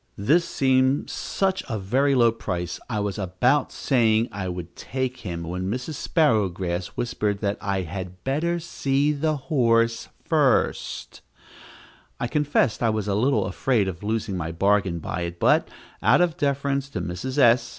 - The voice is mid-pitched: No, low, 115 Hz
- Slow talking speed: No, average, 160 wpm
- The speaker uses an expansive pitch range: Yes, wide, 6.2 semitones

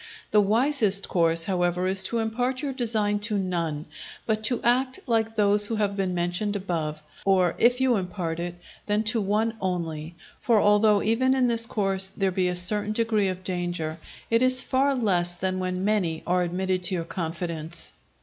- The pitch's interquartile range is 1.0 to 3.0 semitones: No, average, 4.0 semitones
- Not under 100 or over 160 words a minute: No, average, 180 wpm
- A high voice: Yes, high, 195 Hz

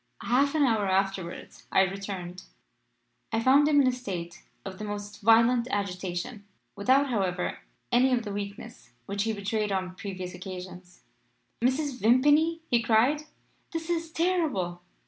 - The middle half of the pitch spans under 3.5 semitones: No, average, 5.3 semitones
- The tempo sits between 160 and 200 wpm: No, average, 145 wpm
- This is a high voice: Yes, high, 215 Hz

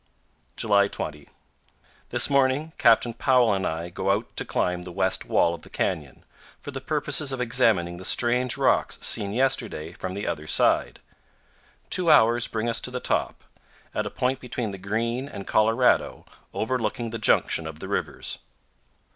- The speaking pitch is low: Yes, low, 115 Hz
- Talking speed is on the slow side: No, average, 165 wpm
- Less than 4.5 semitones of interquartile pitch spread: No, average, 5.0 semitones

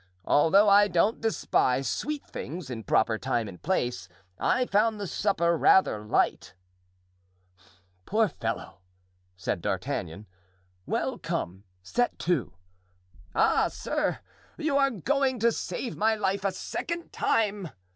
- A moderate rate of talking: No, slow, 125 wpm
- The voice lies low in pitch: No, high, 195 Hz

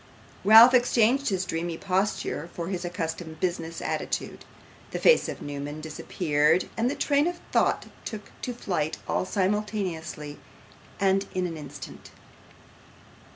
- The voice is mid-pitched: Yes, medium, 180 Hz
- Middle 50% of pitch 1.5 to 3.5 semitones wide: No, average, 4.7 semitones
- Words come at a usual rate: No, slow, 130 wpm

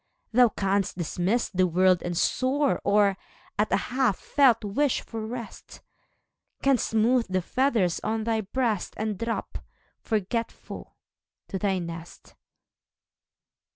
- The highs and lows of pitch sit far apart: No, average, 4.2 semitones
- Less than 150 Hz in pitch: No, high, 215 Hz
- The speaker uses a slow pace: Yes, slow, 120 wpm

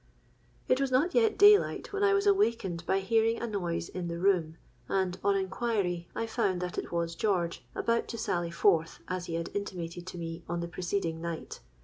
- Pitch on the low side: No, medium, 185 Hz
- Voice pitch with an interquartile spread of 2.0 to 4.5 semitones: No, average, 5.0 semitones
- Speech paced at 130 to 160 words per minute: No, fast, 205 wpm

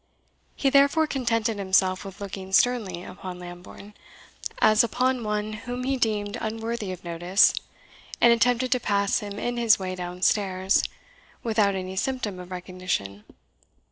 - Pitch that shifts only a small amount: No, average, 4.1 semitones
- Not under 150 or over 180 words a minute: No, average, 140 wpm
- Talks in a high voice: Yes, high, 205 Hz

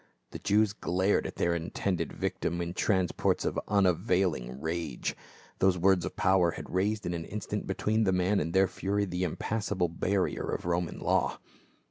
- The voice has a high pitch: No, very low, 90 Hz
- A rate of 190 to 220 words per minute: No, average, 165 wpm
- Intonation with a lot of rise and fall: No, narrow, 2.6 semitones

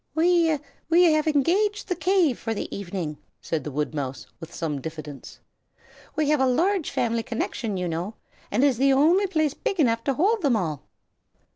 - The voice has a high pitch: Yes, very high, 270 Hz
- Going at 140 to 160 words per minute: No, average, 180 wpm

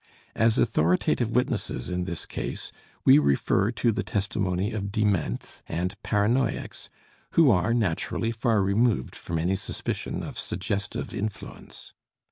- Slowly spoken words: Yes, slow, 125 wpm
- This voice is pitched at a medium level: No, low, 100 Hz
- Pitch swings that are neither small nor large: Yes, average, 3.9 semitones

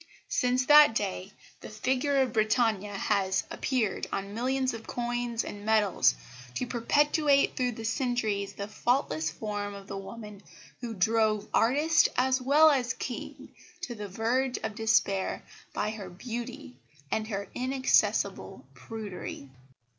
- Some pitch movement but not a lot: Yes, average, 3.8 semitones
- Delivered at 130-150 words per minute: Yes, slow, 135 wpm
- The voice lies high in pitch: Yes, high, 225 Hz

